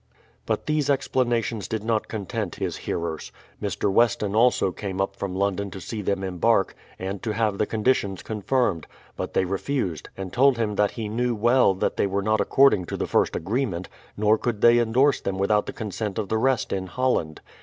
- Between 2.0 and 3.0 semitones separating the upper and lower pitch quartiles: No, average, 3.4 semitones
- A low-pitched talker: Yes, low, 105 Hz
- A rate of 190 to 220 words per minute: Yes, average, 195 wpm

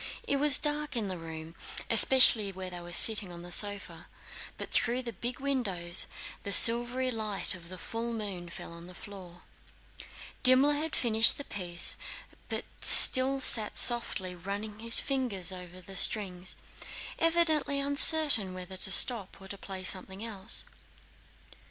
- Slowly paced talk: No, average, 150 wpm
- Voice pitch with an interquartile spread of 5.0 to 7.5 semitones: Yes, wide, 5.6 semitones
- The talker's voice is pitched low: No, high, 205 Hz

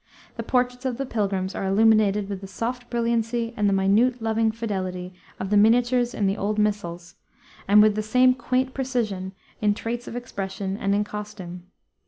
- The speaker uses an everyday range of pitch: Yes, average, 3.4 semitones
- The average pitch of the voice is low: No, high, 215 Hz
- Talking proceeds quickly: No, average, 180 wpm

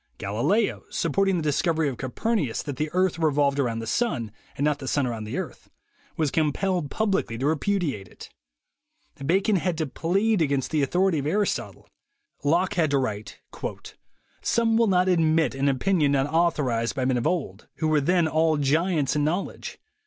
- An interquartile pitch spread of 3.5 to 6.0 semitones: Yes, average, 4.9 semitones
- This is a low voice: No, medium, 155 Hz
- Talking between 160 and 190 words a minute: Yes, average, 180 wpm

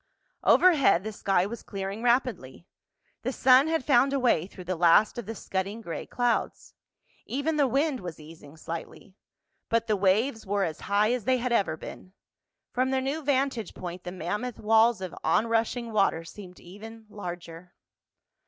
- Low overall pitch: No, high, 215 Hz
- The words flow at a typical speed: Yes, average, 165 wpm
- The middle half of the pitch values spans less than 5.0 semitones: No, wide, 5.4 semitones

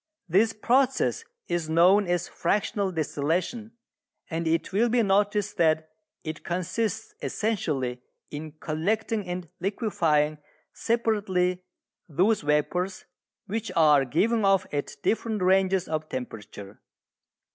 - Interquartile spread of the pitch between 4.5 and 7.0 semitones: Yes, average, 5.1 semitones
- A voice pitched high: No, medium, 180 Hz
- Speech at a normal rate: No, slow, 110 wpm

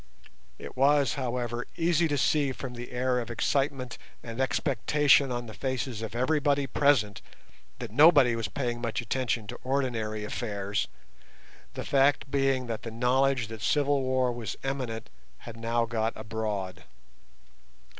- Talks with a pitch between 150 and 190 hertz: No, low, 125 Hz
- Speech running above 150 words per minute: No, average, 145 wpm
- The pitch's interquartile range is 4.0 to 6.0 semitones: No, average, 3.1 semitones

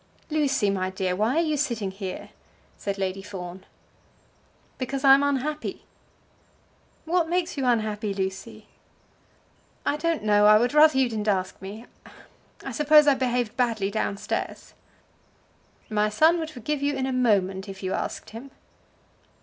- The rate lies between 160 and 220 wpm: No, average, 150 wpm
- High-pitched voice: Yes, high, 230 Hz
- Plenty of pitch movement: Yes, wide, 6.2 semitones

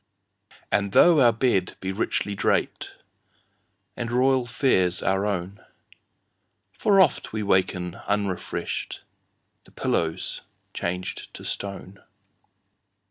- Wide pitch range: No, average, 4.5 semitones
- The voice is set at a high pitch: No, low, 100 Hz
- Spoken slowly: Yes, slow, 85 wpm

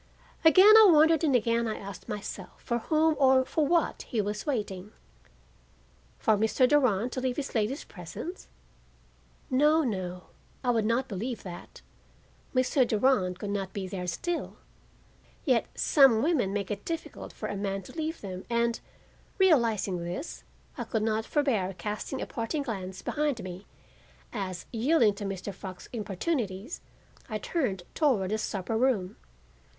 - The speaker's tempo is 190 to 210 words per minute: No, average, 150 wpm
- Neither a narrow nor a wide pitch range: No, wide, 5.7 semitones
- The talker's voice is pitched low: No, high, 225 Hz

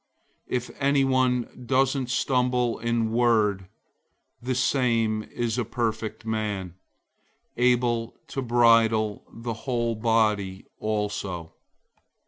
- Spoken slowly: Yes, slow, 95 wpm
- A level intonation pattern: Yes, narrow, 2.3 semitones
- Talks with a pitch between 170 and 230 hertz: No, low, 115 Hz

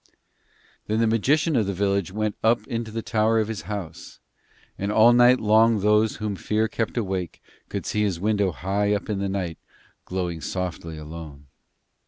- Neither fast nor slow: Yes, average, 175 wpm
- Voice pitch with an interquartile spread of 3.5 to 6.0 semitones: No, average, 2.9 semitones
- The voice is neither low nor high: No, low, 105 Hz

